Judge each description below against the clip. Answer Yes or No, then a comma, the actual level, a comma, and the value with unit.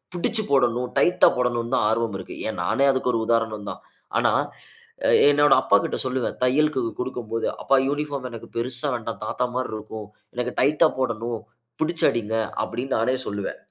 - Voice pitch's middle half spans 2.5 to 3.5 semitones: Yes, average, 2.9 semitones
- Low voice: Yes, low, 125 Hz